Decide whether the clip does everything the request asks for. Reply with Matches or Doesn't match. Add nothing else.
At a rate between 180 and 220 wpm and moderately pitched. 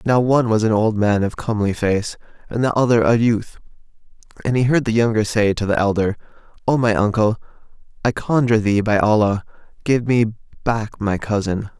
Doesn't match